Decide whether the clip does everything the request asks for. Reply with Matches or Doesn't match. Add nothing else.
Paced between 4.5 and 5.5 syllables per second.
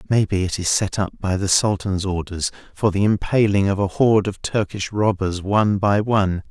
Matches